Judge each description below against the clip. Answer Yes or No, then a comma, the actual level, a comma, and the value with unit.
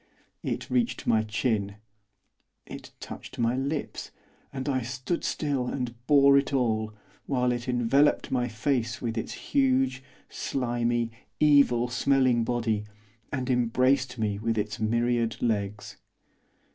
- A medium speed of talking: No, slow, 125 wpm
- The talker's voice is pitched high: No, low, 125 Hz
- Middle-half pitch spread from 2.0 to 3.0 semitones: Yes, narrow, 2.6 semitones